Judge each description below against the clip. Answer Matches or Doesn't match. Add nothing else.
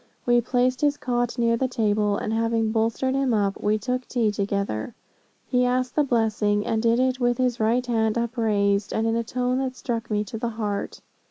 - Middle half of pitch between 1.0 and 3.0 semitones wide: Matches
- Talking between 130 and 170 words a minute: Doesn't match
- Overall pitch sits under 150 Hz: Doesn't match